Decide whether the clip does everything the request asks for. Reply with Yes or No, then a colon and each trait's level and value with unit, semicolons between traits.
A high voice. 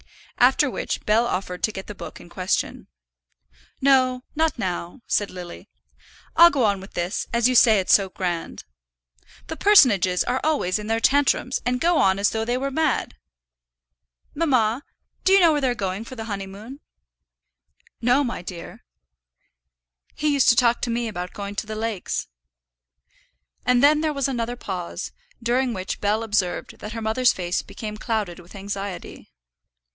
Yes: high, 225 Hz